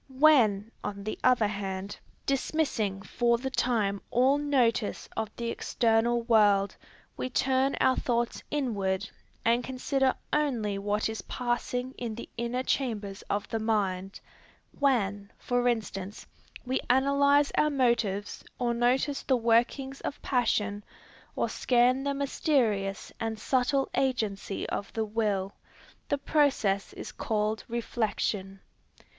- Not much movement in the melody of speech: No, average, 4.0 semitones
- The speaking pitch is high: Yes, high, 235 Hz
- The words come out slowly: Yes, slow, 125 wpm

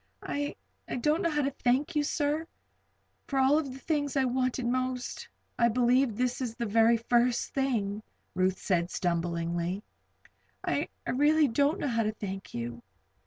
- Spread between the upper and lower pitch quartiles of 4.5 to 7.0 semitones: Yes, average, 5.1 semitones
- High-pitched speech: Yes, very high, 250 Hz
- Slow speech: No, average, 160 wpm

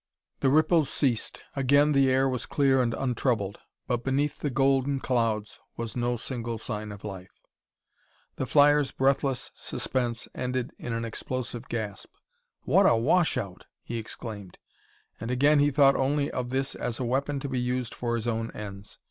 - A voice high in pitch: No, low, 125 Hz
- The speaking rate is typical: Yes, average, 165 wpm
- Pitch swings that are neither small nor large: Yes, average, 3.0 semitones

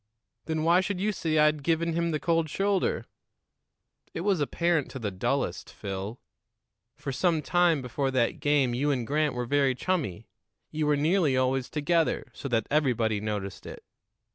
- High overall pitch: No, medium, 150 Hz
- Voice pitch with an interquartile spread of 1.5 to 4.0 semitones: No, average, 4.7 semitones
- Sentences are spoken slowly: No, average, 165 wpm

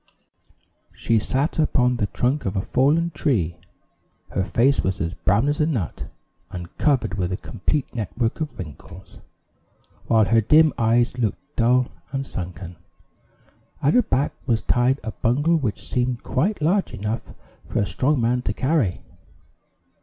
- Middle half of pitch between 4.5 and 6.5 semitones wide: Yes, wide, 5.6 semitones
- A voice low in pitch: Yes, low, 120 Hz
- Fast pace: No, average, 155 wpm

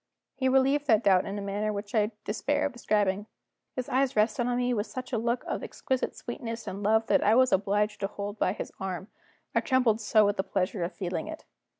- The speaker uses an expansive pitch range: No, average, 3.5 semitones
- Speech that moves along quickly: Yes, fast, 225 wpm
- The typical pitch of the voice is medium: No, high, 215 Hz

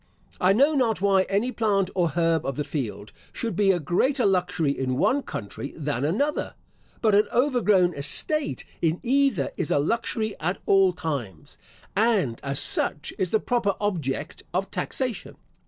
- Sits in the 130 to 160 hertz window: No, high, 190 Hz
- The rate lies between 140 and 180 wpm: Yes, average, 160 wpm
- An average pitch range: No, wide, 7.0 semitones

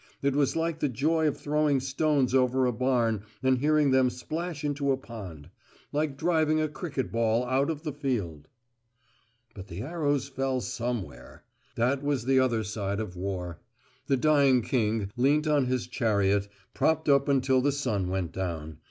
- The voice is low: Yes, low, 130 Hz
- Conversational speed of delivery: Yes, average, 170 wpm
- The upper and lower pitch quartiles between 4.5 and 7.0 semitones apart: Yes, average, 4.8 semitones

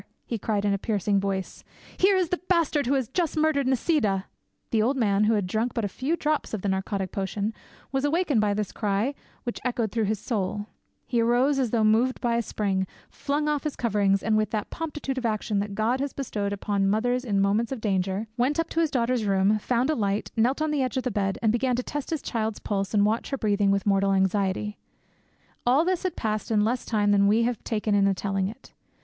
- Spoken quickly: Yes, fast, 230 wpm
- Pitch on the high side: Yes, high, 220 Hz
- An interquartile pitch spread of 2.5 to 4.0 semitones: No, average, 4.5 semitones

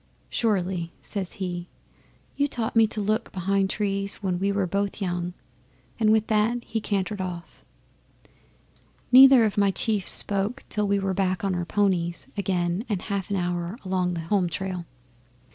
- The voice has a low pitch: No, high, 195 Hz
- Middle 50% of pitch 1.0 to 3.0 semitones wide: Yes, average, 2.7 semitones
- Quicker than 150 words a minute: Yes, average, 160 wpm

